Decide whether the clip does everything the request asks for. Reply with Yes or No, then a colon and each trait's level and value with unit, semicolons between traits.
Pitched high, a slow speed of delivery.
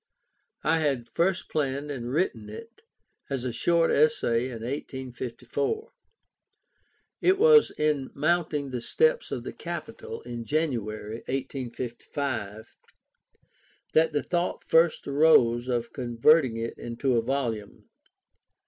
No: low, 135 Hz; slow, 115 wpm